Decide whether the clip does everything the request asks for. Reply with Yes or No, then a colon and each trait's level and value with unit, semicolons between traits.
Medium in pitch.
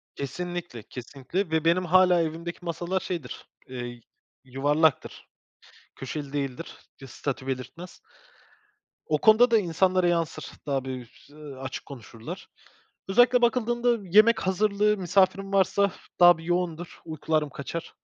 Yes: medium, 170 Hz